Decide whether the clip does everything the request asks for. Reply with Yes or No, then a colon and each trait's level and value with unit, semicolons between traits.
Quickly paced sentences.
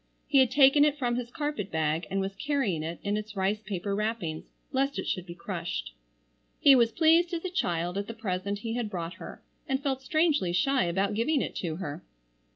Yes: fast, 210 wpm